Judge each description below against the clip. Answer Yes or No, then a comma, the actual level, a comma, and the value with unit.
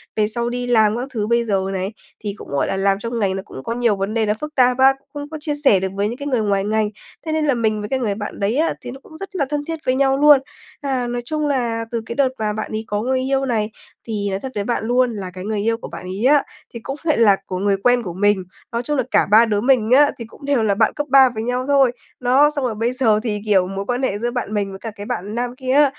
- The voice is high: Yes, high, 235 Hz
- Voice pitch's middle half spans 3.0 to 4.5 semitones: Yes, average, 4.1 semitones